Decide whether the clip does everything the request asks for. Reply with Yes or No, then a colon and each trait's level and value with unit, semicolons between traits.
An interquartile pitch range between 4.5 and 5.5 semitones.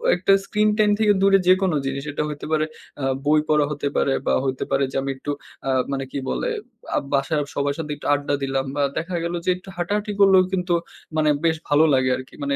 Yes: average, 4.8 semitones